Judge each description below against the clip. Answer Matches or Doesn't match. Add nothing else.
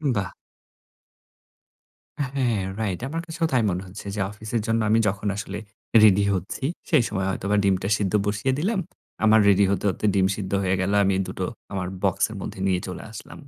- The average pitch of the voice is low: Matches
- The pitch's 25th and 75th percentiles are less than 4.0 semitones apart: Matches